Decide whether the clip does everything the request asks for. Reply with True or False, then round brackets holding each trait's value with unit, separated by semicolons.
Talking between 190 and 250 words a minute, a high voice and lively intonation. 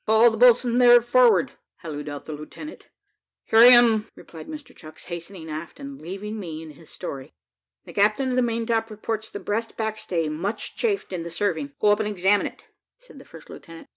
True (200 wpm; 210 Hz; 6.0 semitones)